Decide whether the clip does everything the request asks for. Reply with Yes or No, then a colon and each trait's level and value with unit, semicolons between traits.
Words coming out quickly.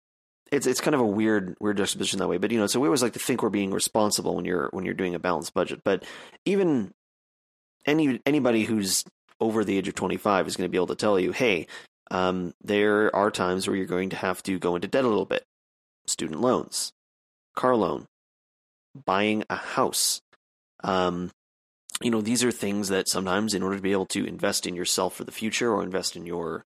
Yes: fast, 215 wpm